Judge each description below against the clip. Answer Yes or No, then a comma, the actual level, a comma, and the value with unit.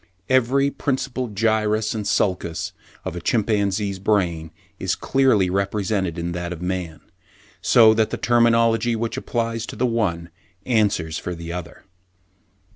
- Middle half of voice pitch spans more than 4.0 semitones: Yes, average, 4.5 semitones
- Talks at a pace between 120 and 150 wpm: Yes, average, 140 wpm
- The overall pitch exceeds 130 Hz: No, low, 105 Hz